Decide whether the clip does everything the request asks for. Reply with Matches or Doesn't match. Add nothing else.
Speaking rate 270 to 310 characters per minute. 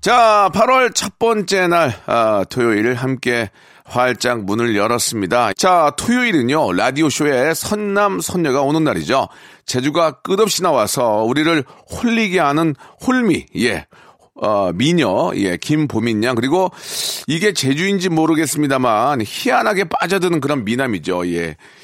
Matches